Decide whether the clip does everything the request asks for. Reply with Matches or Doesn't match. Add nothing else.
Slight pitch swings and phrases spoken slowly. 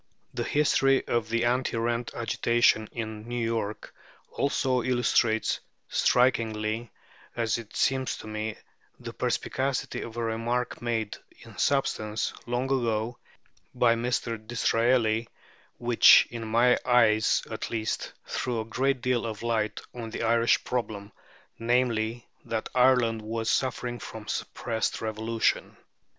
Matches